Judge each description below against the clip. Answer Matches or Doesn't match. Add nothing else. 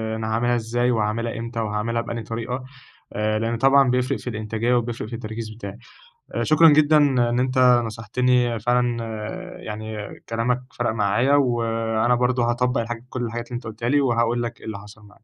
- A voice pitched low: Matches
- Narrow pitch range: Matches